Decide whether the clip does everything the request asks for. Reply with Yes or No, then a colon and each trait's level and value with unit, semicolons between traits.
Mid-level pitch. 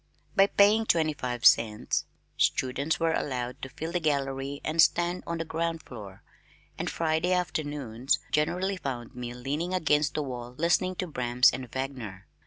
Yes: medium, 145 Hz